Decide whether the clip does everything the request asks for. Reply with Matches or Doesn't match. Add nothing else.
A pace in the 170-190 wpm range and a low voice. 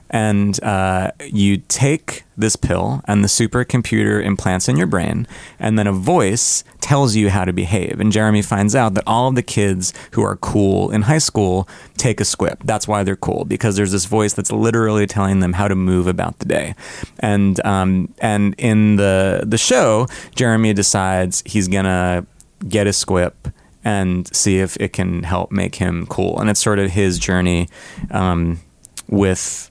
Matches